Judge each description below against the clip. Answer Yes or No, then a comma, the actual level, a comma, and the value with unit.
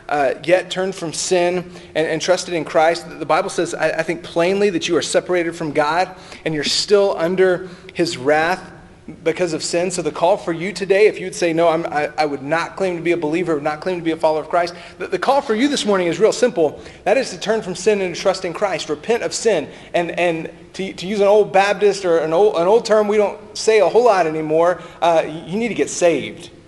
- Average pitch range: Yes, average, 3.0 semitones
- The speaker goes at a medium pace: No, fast, 245 wpm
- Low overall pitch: No, medium, 175 Hz